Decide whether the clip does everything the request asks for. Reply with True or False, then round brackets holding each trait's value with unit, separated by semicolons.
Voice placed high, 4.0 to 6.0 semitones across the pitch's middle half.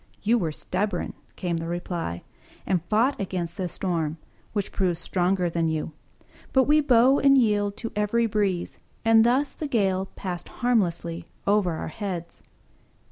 True (195 Hz; 4.6 semitones)